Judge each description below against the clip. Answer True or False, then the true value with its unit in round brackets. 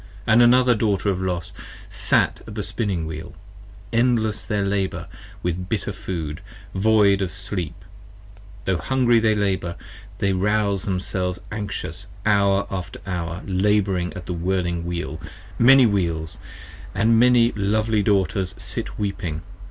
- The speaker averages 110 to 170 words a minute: True (140 wpm)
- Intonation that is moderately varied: True (3.2 semitones)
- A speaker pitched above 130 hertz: False (100 Hz)